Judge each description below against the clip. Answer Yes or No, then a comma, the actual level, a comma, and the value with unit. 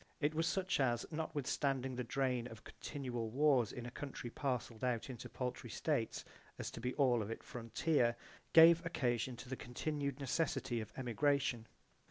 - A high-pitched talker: No, low, 130 Hz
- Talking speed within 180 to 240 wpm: No, average, 165 wpm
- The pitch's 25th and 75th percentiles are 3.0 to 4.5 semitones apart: Yes, average, 3.3 semitones